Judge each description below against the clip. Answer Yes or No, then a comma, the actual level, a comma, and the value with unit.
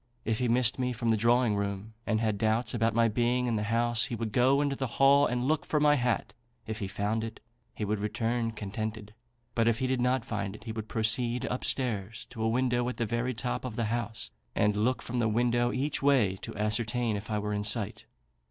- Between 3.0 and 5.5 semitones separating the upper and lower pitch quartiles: No, narrow, 2.5 semitones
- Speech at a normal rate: No, fast, 235 wpm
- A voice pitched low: Yes, low, 115 Hz